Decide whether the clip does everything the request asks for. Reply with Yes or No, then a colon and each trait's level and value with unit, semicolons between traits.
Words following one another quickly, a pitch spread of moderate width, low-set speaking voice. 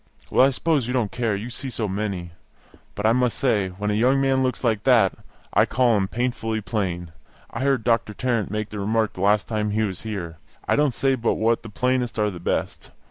Yes: fast, 230 wpm; average, 3.4 semitones; low, 110 Hz